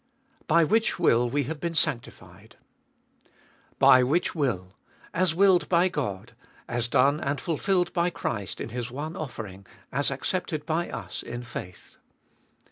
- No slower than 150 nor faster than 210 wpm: No, average, 140 wpm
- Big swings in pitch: Yes, wide, 6.0 semitones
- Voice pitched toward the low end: No, medium, 145 Hz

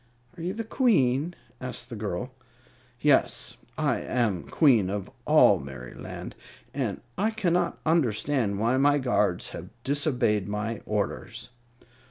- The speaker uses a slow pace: Yes, slow, 125 wpm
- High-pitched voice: No, low, 125 Hz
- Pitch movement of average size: No, wide, 6.2 semitones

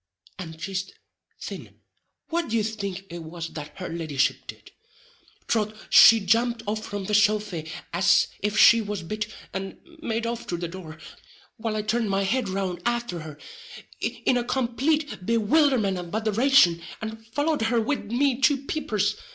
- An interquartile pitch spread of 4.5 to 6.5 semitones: No, average, 4.1 semitones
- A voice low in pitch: No, high, 215 Hz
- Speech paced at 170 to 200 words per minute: No, average, 160 wpm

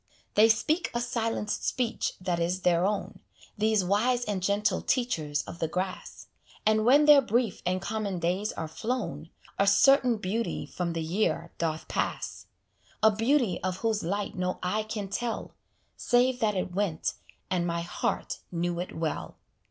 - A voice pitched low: No, high, 205 Hz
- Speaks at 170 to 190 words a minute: No, average, 160 wpm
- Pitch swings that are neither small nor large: Yes, average, 4.3 semitones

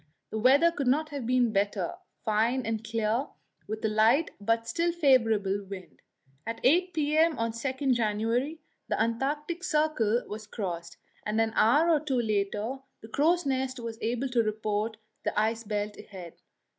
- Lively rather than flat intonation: No, average, 4.5 semitones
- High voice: Yes, high, 230 Hz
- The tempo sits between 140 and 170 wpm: Yes, average, 160 wpm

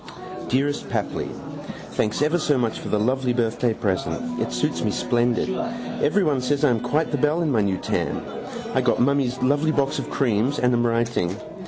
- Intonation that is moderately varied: Yes, average, 3.8 semitones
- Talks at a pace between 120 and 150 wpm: No, average, 185 wpm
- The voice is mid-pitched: No, low, 125 Hz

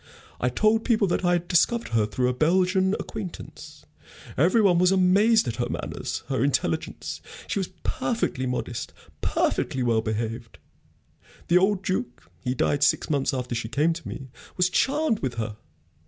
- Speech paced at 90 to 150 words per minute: No, average, 165 wpm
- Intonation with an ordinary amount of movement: No, wide, 7.7 semitones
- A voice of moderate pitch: Yes, medium, 170 Hz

